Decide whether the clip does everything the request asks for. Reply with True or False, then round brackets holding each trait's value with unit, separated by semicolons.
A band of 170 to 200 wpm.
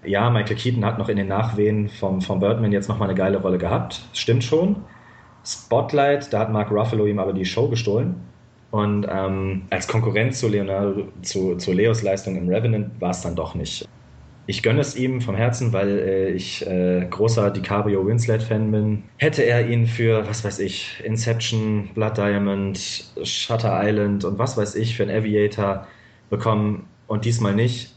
True (180 wpm)